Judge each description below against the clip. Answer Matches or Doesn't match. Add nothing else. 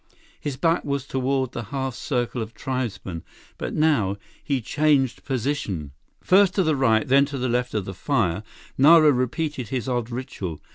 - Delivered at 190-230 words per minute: Doesn't match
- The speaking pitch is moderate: Doesn't match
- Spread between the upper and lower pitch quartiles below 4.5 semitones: Matches